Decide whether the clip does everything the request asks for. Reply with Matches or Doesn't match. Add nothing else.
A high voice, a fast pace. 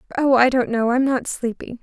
Matches